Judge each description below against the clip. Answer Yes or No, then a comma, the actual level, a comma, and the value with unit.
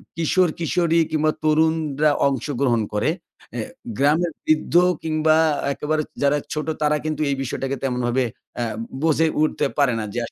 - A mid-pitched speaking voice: Yes, medium, 155 Hz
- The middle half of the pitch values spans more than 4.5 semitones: No, narrow, 2.4 semitones